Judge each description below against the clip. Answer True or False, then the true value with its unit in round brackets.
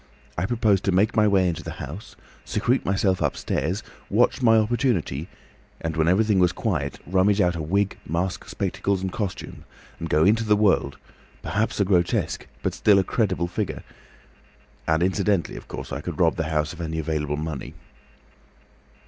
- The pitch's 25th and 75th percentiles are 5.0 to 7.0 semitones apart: False (4.3 semitones)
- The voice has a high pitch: False (95 Hz)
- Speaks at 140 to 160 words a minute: False (170 wpm)